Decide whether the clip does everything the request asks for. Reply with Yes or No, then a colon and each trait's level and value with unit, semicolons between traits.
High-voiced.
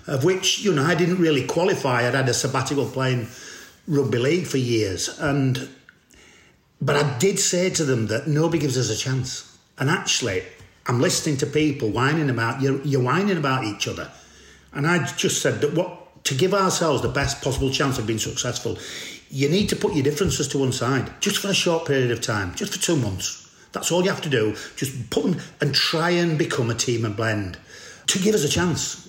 No: medium, 140 Hz